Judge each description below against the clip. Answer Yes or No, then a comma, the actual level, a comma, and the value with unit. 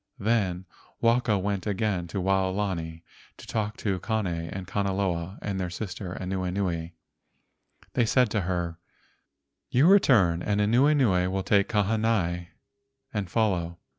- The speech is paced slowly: Yes, slow, 125 wpm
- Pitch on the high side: No, very low, 95 Hz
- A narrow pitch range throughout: No, average, 3.2 semitones